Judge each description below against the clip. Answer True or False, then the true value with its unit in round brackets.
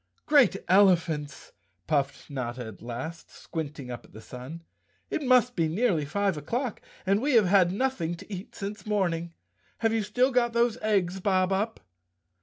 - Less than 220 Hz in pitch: True (190 Hz)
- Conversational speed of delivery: True (160 wpm)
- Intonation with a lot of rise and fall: True (6.0 semitones)